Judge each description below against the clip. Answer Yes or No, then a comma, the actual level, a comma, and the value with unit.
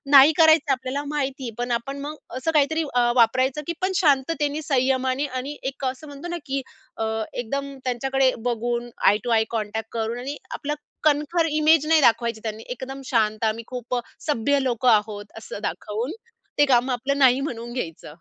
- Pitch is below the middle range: No, very high, 260 Hz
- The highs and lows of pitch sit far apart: No, average, 3.3 semitones